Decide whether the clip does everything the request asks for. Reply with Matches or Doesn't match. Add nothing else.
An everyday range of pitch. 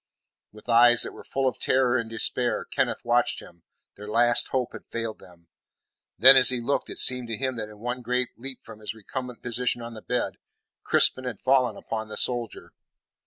Doesn't match